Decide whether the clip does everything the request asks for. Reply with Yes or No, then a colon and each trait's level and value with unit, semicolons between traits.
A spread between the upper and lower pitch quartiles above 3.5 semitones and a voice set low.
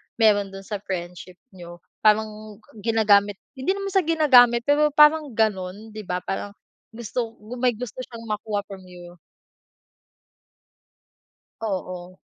No: average, 4.0 semitones; high, 215 Hz